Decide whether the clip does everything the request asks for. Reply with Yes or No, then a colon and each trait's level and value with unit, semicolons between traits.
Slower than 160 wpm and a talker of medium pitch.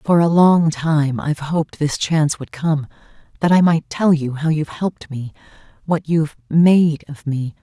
No: average, 190 wpm; medium, 155 Hz